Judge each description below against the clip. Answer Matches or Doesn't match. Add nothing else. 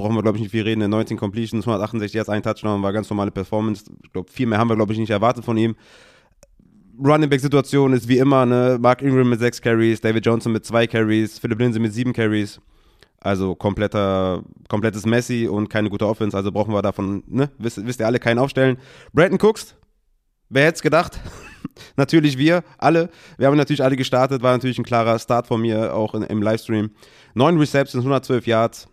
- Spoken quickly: Matches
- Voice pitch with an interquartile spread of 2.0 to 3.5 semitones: Matches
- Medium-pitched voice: Doesn't match